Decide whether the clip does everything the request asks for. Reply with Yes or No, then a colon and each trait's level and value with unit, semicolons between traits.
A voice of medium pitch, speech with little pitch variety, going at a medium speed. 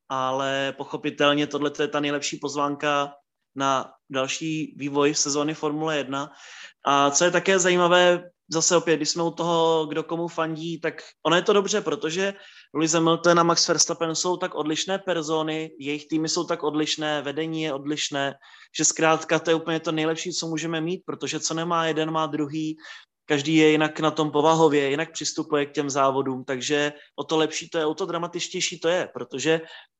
No: medium, 155 Hz; narrow, 2.3 semitones; fast, 180 wpm